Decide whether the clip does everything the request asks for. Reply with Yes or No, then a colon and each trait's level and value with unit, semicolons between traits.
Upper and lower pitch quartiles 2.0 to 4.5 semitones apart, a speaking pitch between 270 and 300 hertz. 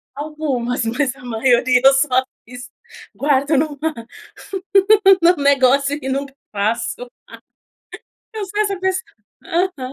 Yes: average, 3.7 semitones; very high, 275 Hz